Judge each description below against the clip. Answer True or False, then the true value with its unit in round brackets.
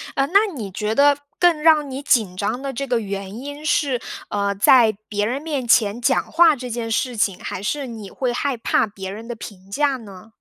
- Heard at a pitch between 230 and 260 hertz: True (240 Hz)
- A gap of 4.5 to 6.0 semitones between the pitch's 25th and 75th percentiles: True (5.3 semitones)